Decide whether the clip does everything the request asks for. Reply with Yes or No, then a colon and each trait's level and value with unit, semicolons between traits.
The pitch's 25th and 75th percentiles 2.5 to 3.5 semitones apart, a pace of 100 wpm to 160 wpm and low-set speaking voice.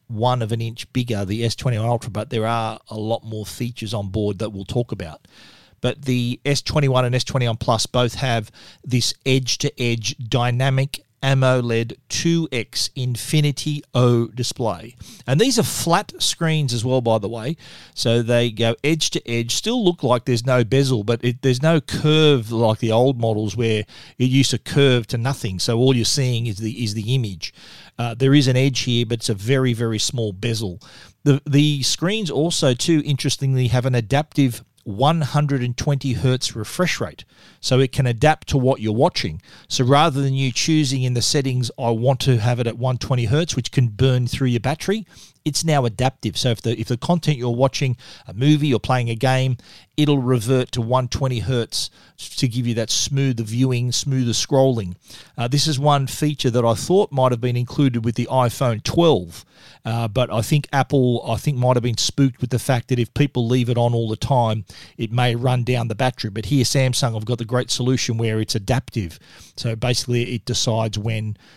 No: average, 2.8 semitones; average, 190 wpm; low, 125 Hz